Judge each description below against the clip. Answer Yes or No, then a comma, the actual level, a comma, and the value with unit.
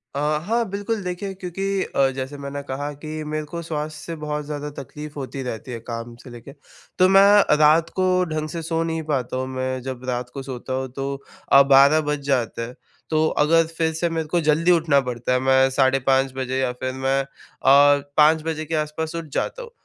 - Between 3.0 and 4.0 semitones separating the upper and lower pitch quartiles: Yes, average, 3.5 semitones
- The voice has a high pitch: No, medium, 145 Hz